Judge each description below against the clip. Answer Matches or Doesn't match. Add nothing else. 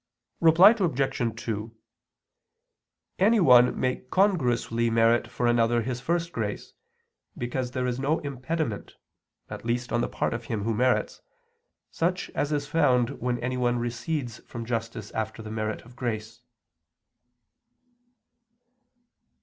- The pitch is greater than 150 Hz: Doesn't match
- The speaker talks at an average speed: Doesn't match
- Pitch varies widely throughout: Doesn't match